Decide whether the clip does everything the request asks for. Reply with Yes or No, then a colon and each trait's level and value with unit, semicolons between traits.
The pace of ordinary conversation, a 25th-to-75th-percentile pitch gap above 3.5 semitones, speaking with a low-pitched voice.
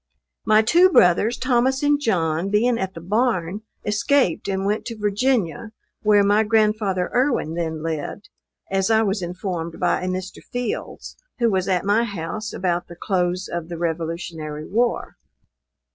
No: average, 155 wpm; average, 4.4 semitones; high, 195 Hz